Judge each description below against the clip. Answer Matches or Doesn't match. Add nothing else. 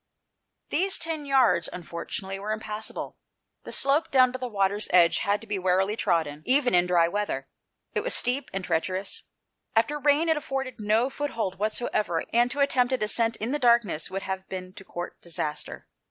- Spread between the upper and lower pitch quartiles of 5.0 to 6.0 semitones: Matches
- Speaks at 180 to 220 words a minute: Matches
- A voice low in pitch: Doesn't match